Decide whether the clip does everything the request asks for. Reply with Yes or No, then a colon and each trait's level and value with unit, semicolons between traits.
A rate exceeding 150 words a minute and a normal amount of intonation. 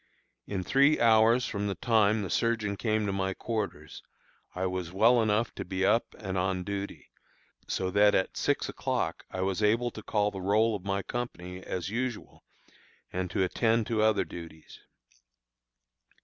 Yes: average, 165 wpm; average, 3.1 semitones